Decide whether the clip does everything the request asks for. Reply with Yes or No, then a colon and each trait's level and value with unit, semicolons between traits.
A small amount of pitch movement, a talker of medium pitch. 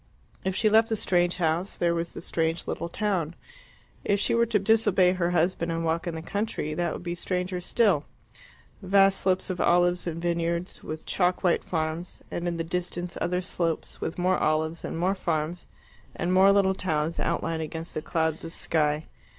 Yes: narrow, 2.2 semitones; medium, 175 Hz